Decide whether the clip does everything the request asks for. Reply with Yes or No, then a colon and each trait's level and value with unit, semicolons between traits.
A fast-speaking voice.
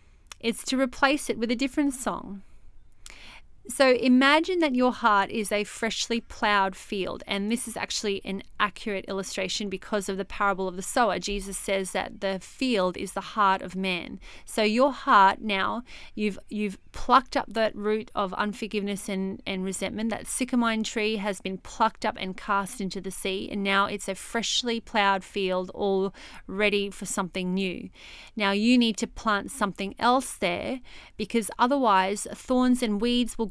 No: average, 170 wpm